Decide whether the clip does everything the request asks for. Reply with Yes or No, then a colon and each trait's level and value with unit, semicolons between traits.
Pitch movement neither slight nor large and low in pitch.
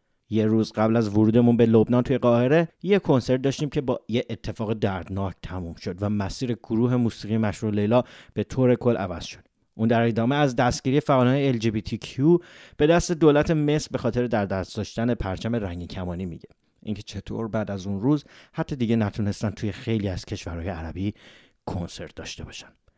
Yes: average, 3.9 semitones; low, 115 Hz